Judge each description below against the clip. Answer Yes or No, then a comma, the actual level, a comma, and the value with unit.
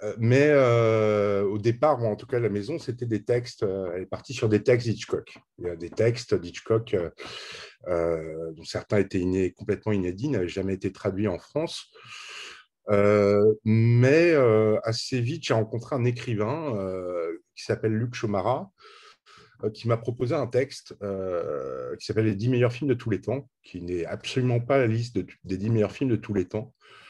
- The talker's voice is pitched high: No, low, 110 Hz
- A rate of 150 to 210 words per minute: Yes, average, 195 wpm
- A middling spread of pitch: Yes, average, 3.7 semitones